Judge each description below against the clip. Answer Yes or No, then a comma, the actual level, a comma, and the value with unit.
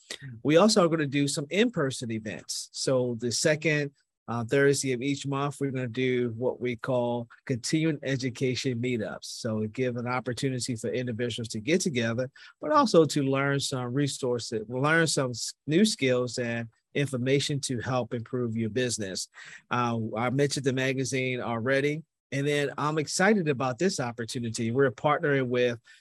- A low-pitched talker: Yes, low, 130 Hz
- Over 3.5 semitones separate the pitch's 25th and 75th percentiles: No, average, 2.7 semitones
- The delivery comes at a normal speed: Yes, average, 165 wpm